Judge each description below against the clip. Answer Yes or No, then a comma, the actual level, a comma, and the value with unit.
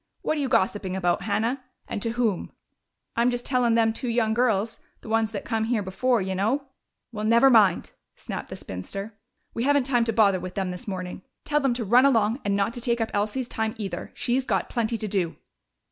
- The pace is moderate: No, fast, 220 wpm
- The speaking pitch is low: No, high, 225 Hz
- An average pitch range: Yes, average, 3.3 semitones